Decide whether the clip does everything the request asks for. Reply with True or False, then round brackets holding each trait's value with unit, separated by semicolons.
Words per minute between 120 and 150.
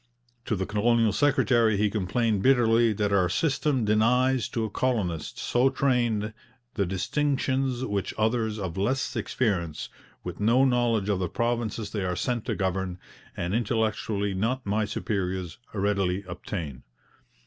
True (140 wpm)